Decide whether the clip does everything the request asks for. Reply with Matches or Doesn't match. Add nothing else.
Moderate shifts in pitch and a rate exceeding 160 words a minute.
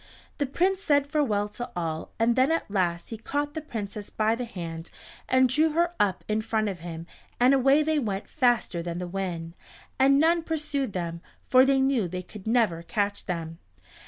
Doesn't match